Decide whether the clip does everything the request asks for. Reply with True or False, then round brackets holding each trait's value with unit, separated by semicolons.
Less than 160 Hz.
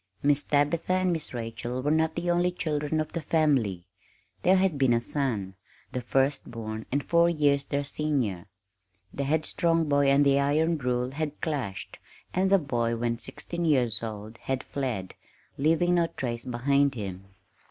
True (140 Hz)